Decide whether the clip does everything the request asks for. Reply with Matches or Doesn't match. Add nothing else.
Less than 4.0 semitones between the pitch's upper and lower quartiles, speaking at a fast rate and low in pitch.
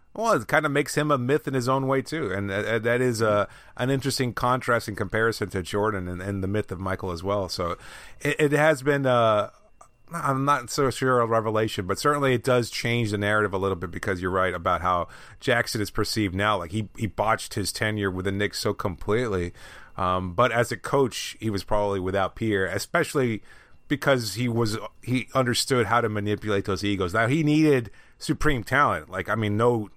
Doesn't match